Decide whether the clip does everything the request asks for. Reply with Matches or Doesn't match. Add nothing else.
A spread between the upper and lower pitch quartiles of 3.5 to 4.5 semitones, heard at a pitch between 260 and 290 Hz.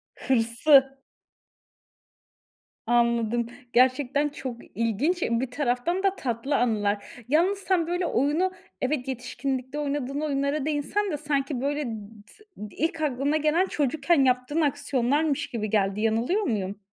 Matches